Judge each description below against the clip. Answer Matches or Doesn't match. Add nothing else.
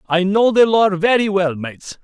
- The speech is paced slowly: Doesn't match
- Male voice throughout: Matches